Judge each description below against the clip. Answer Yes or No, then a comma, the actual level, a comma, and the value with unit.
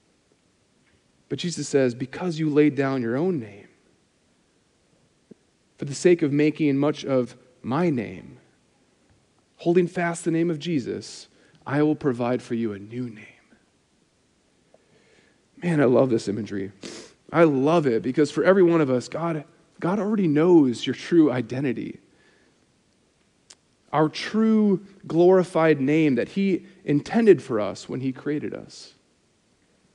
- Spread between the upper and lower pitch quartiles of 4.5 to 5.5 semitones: Yes, average, 4.9 semitones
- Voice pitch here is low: No, medium, 150 Hz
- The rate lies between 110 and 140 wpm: Yes, slow, 135 wpm